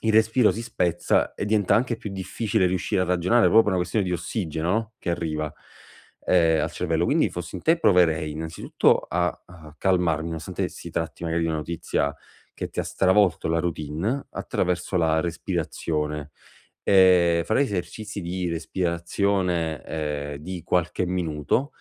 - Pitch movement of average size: Yes, average, 3.1 semitones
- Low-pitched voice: Yes, very low, 85 Hz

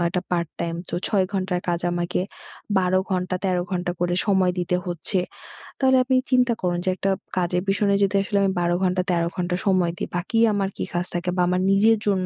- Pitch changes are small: Yes, narrow, 1.9 semitones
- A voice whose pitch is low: No, medium, 185 Hz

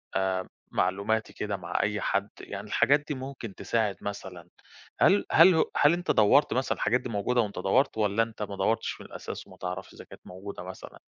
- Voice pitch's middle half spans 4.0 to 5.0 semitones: Yes, average, 4.3 semitones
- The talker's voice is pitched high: No, low, 105 Hz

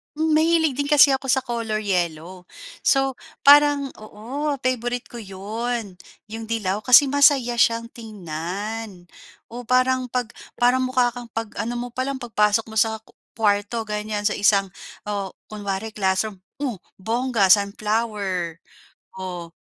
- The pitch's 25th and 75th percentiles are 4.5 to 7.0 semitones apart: No, average, 3.8 semitones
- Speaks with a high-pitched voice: Yes, high, 225 Hz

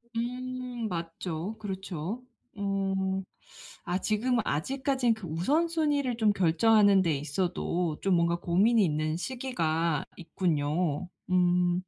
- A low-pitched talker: No, high, 190 Hz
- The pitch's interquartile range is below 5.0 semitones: No, wide, 5.5 semitones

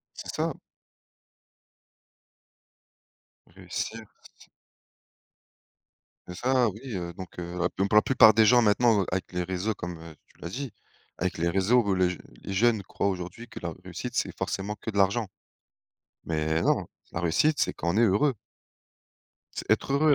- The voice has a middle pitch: No, very low, 95 Hz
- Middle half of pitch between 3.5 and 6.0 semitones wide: Yes, average, 4.2 semitones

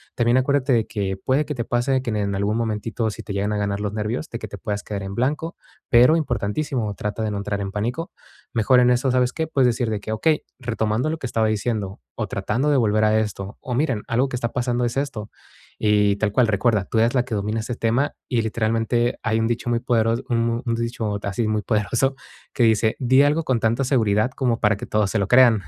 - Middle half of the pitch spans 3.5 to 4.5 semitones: No, average, 2.9 semitones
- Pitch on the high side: No, low, 115 Hz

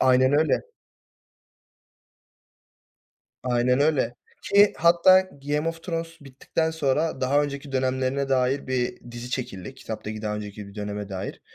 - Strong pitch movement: No, average, 3.9 semitones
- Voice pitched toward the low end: Yes, low, 130 Hz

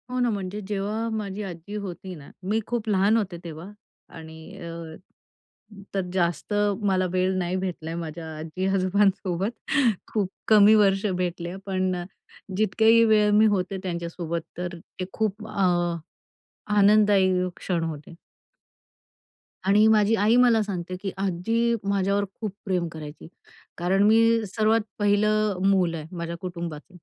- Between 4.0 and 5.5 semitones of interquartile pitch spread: No, average, 3.3 semitones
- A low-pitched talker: No, high, 190 Hz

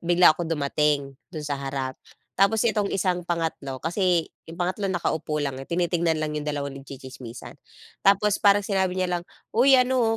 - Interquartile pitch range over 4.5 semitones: Yes, average, 5.1 semitones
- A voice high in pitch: No, medium, 170 Hz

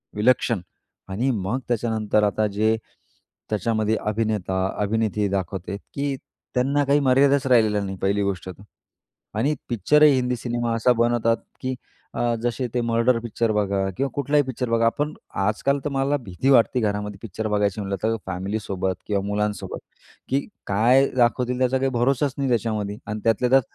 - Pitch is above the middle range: No, low, 115 Hz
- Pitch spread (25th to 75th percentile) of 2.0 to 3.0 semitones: No, average, 3.6 semitones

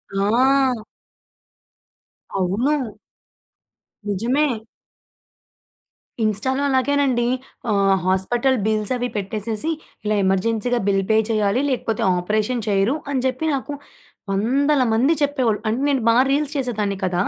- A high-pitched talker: Yes, high, 230 Hz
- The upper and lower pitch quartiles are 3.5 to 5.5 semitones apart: Yes, average, 4.2 semitones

